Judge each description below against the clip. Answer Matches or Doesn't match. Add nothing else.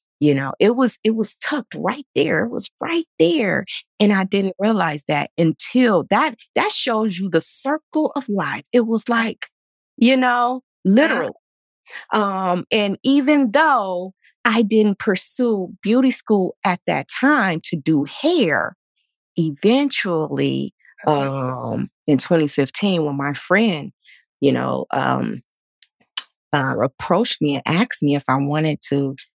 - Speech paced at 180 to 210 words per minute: Doesn't match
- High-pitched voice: Matches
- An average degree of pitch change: Doesn't match